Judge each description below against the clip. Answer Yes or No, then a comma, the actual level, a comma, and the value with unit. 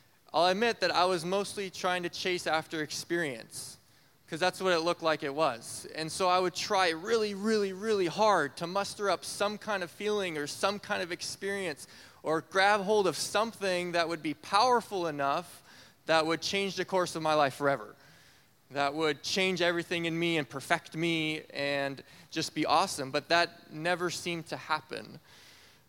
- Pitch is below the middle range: No, medium, 170 Hz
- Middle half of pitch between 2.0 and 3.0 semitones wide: No, average, 3.7 semitones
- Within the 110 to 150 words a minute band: No, average, 180 wpm